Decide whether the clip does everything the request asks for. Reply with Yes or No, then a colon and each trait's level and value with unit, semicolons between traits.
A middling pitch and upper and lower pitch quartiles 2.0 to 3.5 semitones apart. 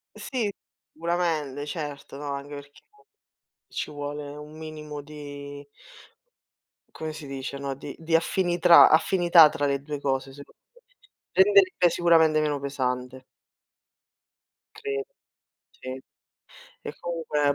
Yes: medium, 150 Hz; average, 2.8 semitones